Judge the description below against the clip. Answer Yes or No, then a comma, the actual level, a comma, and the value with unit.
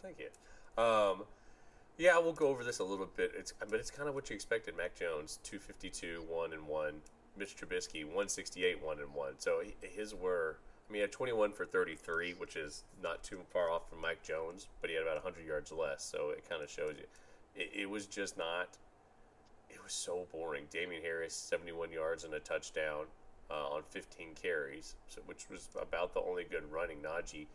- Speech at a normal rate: No, fast, 215 wpm